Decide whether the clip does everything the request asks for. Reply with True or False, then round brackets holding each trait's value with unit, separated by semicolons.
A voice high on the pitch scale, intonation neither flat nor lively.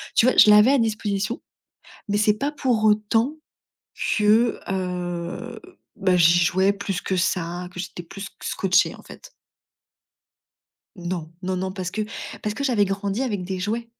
True (200 Hz; 3.1 semitones)